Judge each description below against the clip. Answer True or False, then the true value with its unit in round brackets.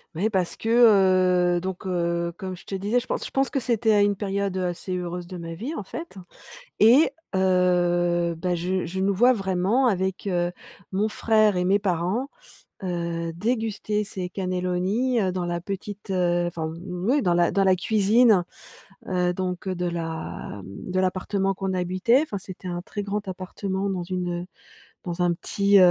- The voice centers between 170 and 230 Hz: True (185 Hz)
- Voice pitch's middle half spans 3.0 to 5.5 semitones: False (2.5 semitones)